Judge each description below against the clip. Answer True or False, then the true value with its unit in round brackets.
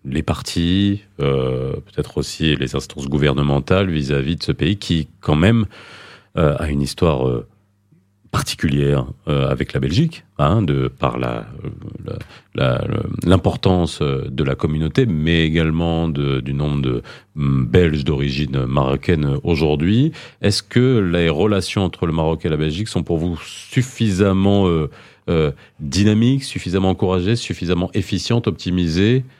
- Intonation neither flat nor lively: False (5.7 semitones)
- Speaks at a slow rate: True (135 wpm)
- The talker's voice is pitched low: True (85 Hz)